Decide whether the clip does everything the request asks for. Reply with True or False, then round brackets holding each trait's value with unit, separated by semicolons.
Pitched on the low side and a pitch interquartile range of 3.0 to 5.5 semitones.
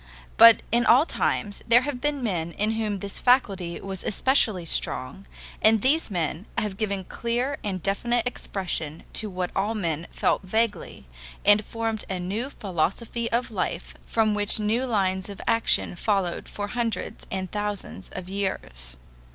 False (205 Hz; 3.6 semitones)